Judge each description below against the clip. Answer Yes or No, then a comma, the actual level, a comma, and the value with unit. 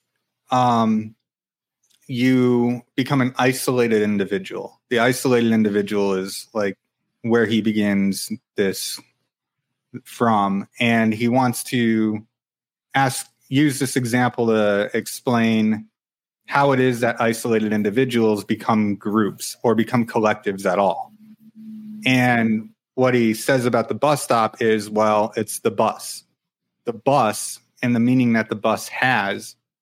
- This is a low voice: Yes, low, 115 Hz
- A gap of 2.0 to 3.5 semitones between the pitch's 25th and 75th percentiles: Yes, narrow, 2.6 semitones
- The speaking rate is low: Yes, slow, 125 wpm